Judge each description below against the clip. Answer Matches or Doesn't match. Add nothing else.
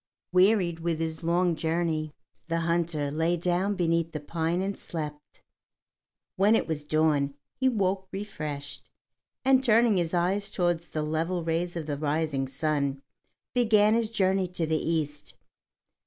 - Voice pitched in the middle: Matches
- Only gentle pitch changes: Doesn't match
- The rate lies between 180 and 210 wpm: Doesn't match